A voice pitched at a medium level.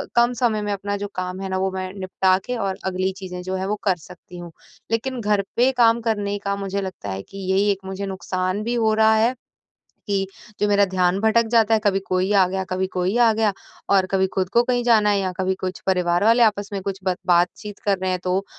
No: high, 195 Hz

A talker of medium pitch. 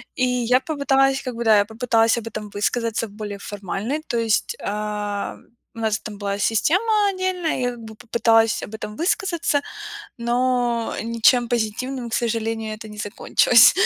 No: high, 230 Hz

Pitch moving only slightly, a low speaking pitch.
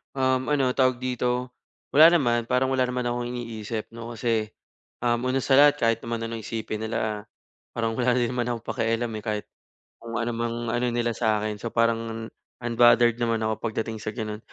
Yes: narrow, 1.6 semitones; low, 120 Hz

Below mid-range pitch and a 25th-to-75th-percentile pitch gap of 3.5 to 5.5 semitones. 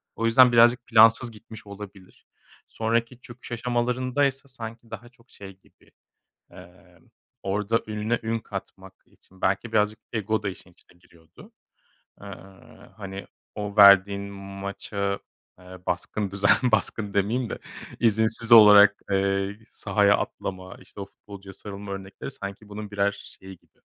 No: low, 105 Hz; average, 2.7 semitones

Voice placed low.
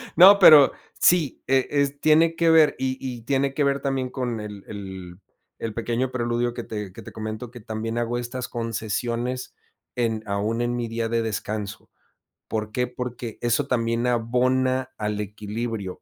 Yes: low, 120 Hz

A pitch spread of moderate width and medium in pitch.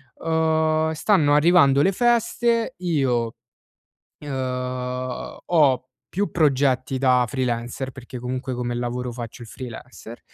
No: average, 4.1 semitones; low, 130 Hz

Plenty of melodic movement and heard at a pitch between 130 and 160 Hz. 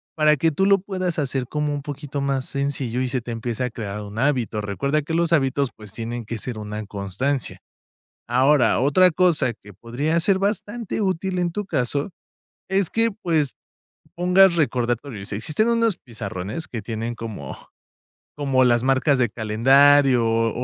Yes: wide, 6.0 semitones; low, 135 Hz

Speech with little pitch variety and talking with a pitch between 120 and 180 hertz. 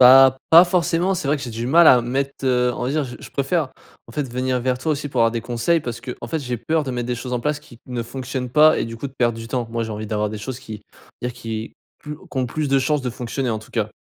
No: average, 3.1 semitones; low, 125 Hz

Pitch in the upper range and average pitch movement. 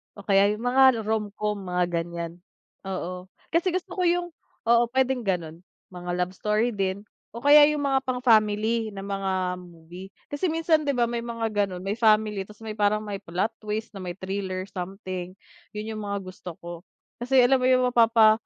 Yes: high, 210 Hz; average, 4.1 semitones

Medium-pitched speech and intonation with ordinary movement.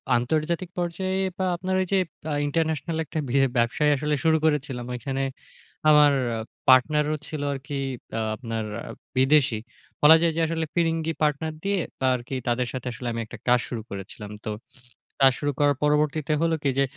Yes: medium, 150 Hz; average, 3.9 semitones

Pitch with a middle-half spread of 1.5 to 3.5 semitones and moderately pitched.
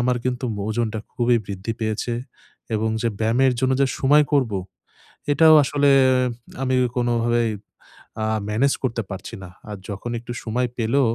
No: average, 2.8 semitones; low, 120 Hz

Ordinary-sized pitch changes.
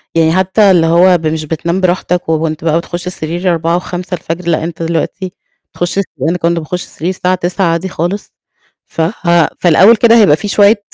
No: narrow, 2.2 semitones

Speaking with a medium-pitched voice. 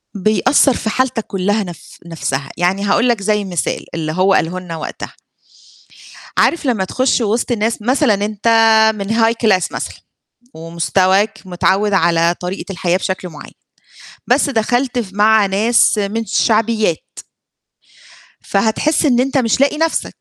No: high, 205 Hz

